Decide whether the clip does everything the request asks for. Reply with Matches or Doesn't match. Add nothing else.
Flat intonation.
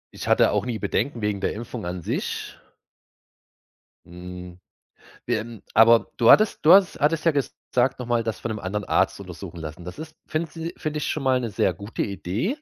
Doesn't match